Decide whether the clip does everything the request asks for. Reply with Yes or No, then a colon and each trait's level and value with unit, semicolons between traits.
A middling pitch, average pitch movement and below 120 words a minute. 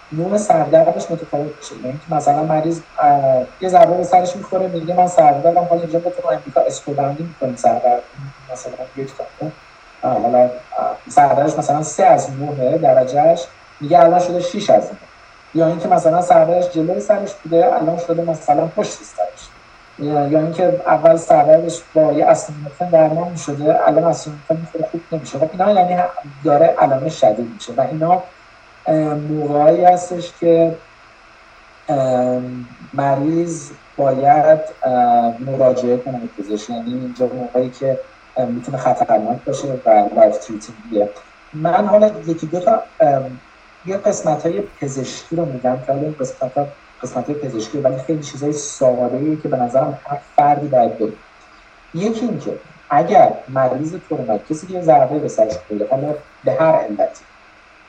No: medium, 155 Hz; average, 4.5 semitones; average, 130 wpm